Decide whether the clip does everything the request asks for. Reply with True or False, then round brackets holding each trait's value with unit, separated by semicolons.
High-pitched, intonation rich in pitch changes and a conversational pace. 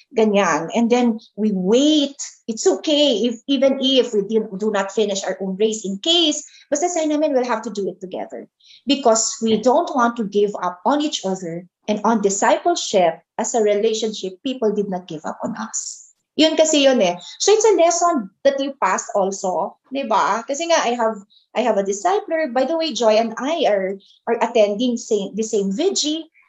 False (225 Hz; 5.7 semitones; 195 wpm)